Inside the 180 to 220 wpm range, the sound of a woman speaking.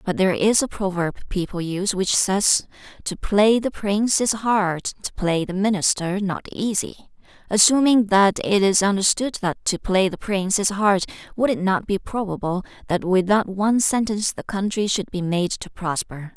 Yes: average, 185 wpm; female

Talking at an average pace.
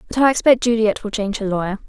No: fast, 255 wpm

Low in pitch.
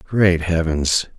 Yes: very low, 85 Hz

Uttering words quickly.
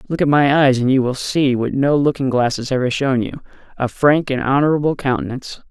Yes: fast, 210 wpm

